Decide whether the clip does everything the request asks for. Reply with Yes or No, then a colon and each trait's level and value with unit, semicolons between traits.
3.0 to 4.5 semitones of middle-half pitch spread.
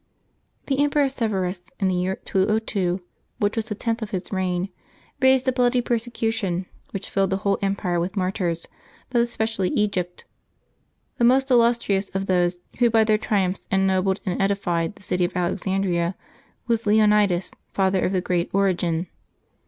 Yes: average, 3.5 semitones